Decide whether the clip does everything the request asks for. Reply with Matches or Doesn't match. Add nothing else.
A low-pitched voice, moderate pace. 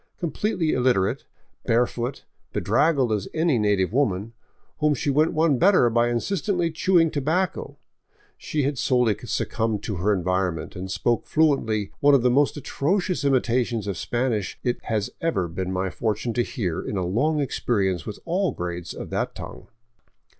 Matches